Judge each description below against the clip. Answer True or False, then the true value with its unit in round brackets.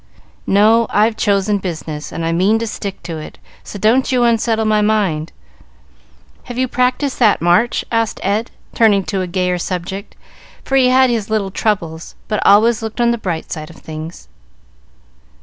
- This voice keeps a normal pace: True (170 wpm)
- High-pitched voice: True (210 Hz)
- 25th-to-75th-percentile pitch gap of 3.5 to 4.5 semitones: True (4.1 semitones)